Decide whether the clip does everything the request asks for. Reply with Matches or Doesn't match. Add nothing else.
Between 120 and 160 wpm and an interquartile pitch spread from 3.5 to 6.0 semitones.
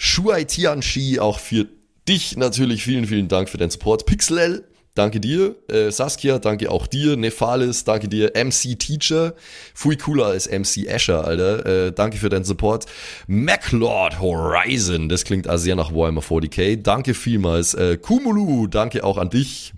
Matches